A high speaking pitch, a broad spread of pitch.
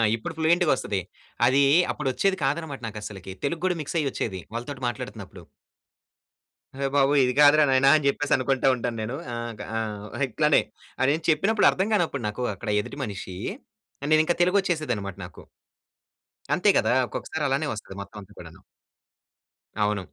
No: low, 135 Hz; wide, 6.0 semitones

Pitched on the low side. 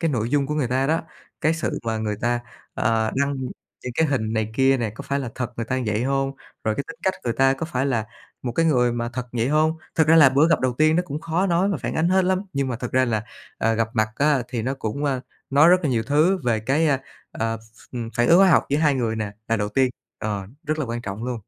Yes: low, 130 Hz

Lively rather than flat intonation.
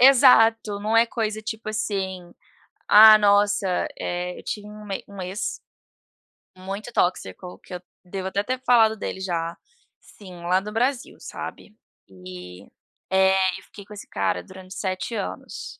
No: average, 2.8 semitones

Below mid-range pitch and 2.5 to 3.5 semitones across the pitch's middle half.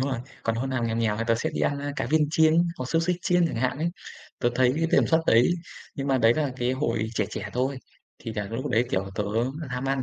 No: low, 130 Hz; average, 4.3 semitones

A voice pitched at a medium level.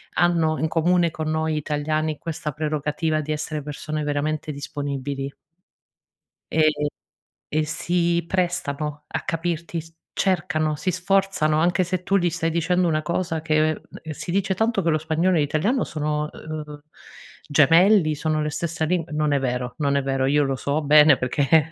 Yes: medium, 155 Hz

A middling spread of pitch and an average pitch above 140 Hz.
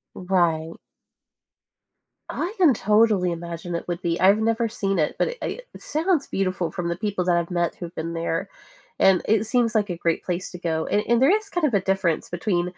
Yes: average, 4.4 semitones; medium, 185 Hz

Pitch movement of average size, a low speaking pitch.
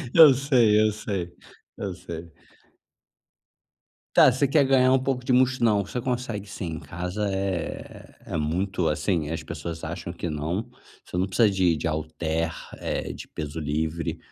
No: wide, 6.4 semitones; very low, 95 Hz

